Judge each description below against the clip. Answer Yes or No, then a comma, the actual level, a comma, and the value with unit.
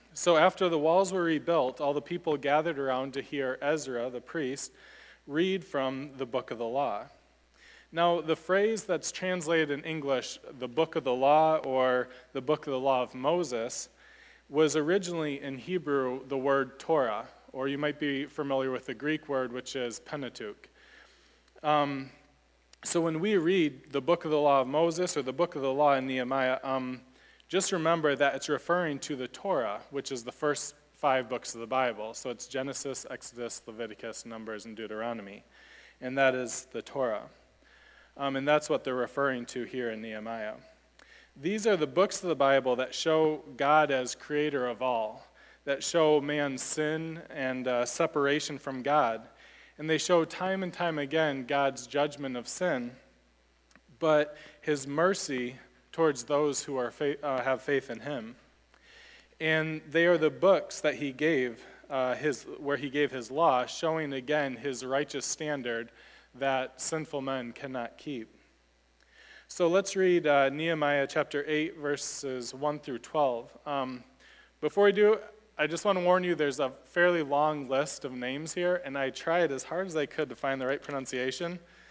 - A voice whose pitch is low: No, medium, 145 Hz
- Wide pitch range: No, average, 3.6 semitones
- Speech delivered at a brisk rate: No, average, 175 wpm